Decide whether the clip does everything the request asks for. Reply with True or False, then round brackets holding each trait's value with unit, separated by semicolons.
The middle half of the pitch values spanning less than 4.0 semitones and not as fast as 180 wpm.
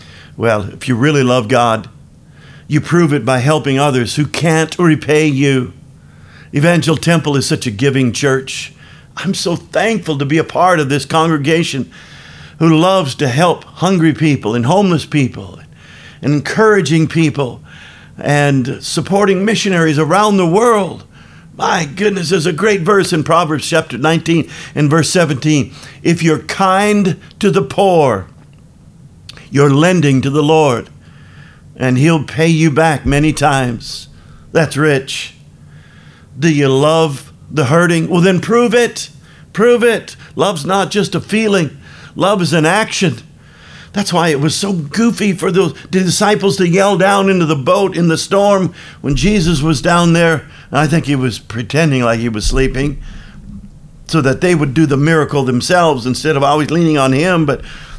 False (4.5 semitones; 155 wpm)